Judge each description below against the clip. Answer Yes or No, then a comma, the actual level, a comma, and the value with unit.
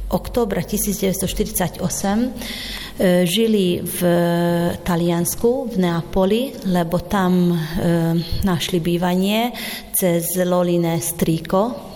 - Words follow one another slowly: Yes, slow, 85 wpm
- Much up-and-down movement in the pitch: No, average, 3.5 semitones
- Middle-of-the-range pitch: Yes, medium, 180 Hz